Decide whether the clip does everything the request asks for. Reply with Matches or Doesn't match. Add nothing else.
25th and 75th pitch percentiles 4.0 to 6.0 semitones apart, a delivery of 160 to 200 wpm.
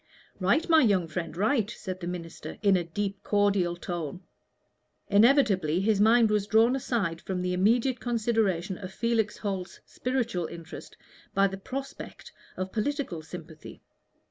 Doesn't match